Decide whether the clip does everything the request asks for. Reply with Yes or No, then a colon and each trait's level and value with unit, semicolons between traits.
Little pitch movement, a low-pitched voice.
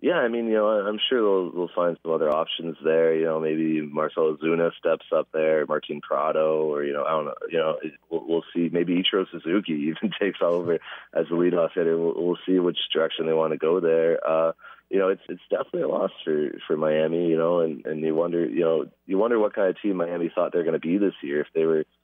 Yes: narrow, 1.6 semitones; very low, 80 Hz